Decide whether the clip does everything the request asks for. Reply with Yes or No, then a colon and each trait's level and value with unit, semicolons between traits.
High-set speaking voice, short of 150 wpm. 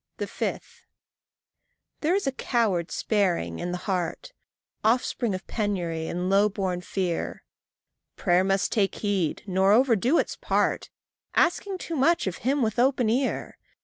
Yes: high, 205 Hz; average, 140 wpm